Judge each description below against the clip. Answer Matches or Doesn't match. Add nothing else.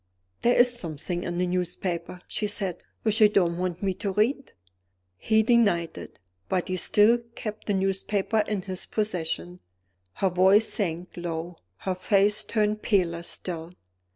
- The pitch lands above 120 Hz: Matches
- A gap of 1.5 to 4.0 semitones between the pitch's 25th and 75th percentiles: Matches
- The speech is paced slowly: Doesn't match